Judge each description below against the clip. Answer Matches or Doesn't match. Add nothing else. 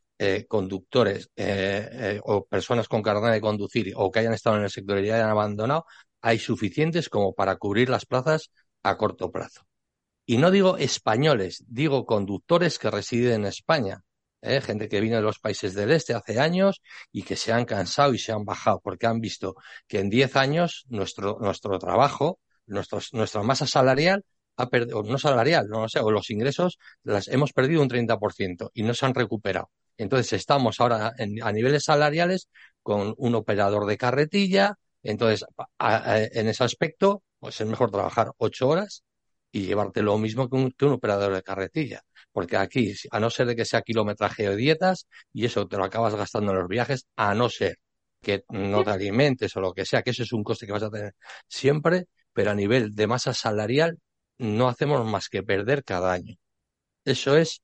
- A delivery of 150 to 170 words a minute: Doesn't match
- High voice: Doesn't match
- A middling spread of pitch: Matches